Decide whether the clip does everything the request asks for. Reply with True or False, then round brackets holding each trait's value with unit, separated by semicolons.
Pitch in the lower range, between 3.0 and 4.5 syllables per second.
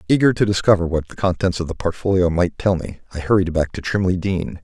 False (90 Hz; 6.0 syllables/s)